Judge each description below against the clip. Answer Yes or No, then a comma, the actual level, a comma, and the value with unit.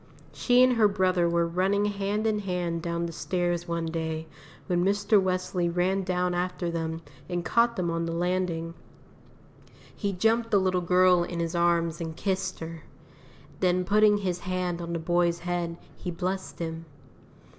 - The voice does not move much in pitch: Yes, narrow, 2.0 semitones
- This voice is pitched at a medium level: Yes, medium, 180 Hz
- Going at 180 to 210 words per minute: No, average, 165 wpm